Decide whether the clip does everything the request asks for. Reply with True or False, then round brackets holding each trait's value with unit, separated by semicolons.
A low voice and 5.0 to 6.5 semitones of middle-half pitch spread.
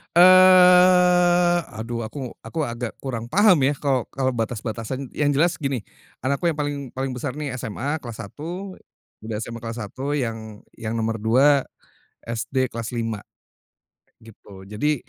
True (130 Hz; 5.4 semitones)